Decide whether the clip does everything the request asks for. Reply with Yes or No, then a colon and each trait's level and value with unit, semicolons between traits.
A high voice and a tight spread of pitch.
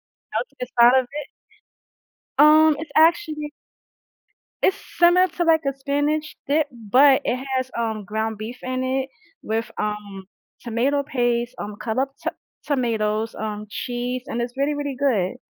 No: very high, 255 Hz; average, 4.2 semitones